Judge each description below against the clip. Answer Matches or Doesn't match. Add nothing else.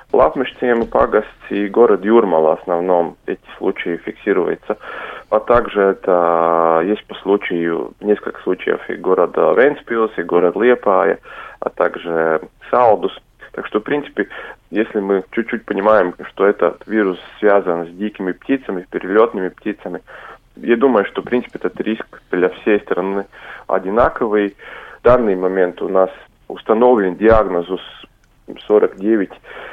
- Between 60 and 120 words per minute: Doesn't match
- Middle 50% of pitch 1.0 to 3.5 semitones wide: Doesn't match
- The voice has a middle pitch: Doesn't match